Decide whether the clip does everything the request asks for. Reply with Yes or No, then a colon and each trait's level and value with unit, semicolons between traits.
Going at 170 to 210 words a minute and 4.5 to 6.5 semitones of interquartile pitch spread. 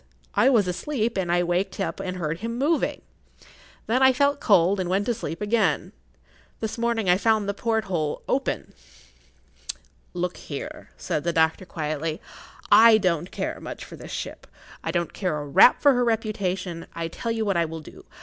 Yes: average, 180 wpm; average, 4.9 semitones